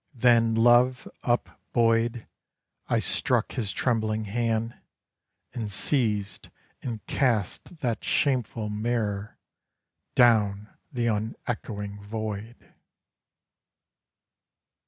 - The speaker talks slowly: Yes, slow, 75 wpm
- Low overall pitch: Yes, low, 115 Hz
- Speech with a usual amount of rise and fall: No, narrow, 2.3 semitones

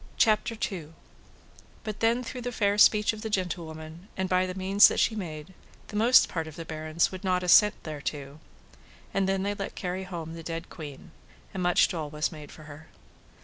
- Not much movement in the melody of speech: No, average, 4.1 semitones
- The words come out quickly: No, average, 190 wpm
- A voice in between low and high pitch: Yes, medium, 180 Hz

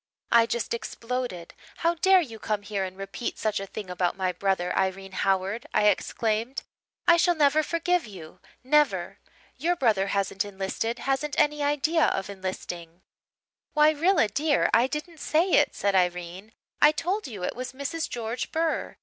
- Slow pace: No, average, 165 wpm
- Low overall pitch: No, high, 230 Hz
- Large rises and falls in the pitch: Yes, wide, 7.7 semitones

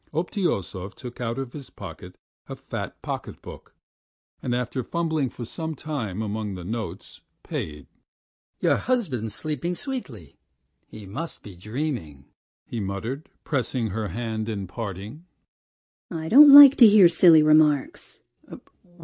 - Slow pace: Yes, slow, 130 wpm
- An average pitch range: No, wide, 7.1 semitones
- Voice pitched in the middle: No, low, 125 Hz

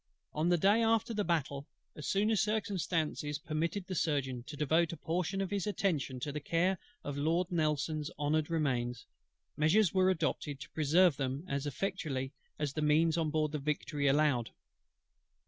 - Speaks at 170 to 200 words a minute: Yes, average, 175 wpm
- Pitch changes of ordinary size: Yes, average, 3.8 semitones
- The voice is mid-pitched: Yes, medium, 155 Hz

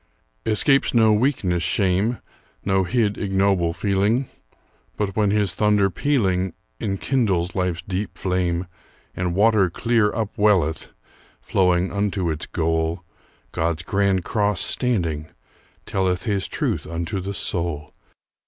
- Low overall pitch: Yes, very low, 95 Hz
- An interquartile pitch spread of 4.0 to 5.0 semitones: No, average, 3.0 semitones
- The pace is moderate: No, slow, 115 wpm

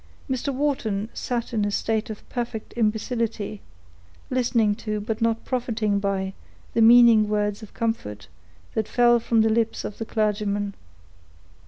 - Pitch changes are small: Yes, narrow, 2.1 semitones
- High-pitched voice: Yes, high, 220 Hz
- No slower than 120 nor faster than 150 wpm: Yes, average, 145 wpm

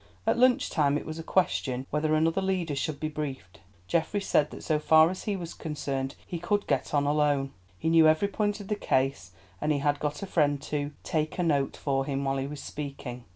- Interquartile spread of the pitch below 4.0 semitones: Yes, average, 3.0 semitones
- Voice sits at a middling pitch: Yes, medium, 150 Hz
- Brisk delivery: Yes, fast, 225 wpm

